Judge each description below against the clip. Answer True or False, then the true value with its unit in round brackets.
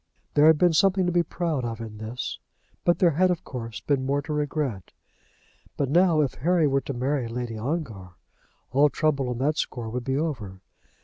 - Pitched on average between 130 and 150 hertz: True (140 Hz)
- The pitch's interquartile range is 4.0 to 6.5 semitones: True (4.9 semitones)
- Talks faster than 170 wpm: True (195 wpm)